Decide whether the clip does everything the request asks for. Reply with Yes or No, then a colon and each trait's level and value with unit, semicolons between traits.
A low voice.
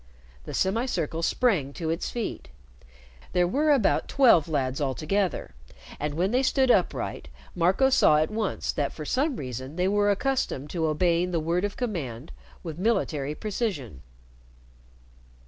No: medium, 175 Hz